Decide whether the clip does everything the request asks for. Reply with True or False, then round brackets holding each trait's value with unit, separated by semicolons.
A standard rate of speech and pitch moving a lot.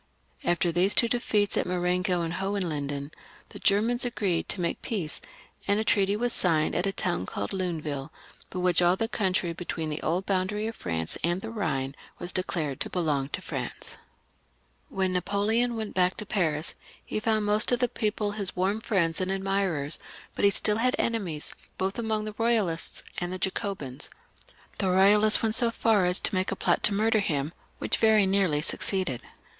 False (180 wpm; 3.8 semitones)